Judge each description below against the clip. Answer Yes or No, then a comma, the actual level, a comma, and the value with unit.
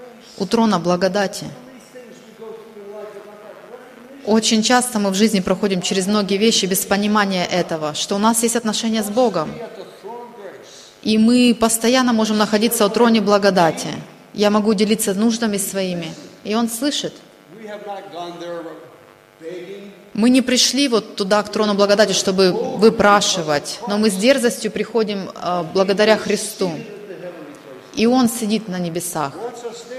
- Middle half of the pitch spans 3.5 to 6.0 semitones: No, average, 2.9 semitones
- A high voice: Yes, high, 210 Hz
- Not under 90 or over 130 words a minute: Yes, average, 120 wpm